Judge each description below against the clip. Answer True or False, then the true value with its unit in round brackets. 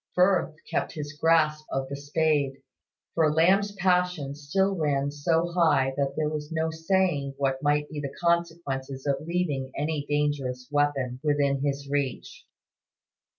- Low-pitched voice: False (150 Hz)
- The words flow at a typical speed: True (145 wpm)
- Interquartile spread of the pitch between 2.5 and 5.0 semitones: True (2.9 semitones)